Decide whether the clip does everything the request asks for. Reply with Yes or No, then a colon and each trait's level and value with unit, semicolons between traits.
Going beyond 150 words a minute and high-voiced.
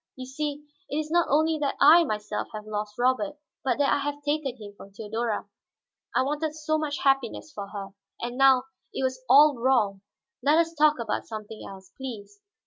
Yes: average, 190 wpm; very high, 265 Hz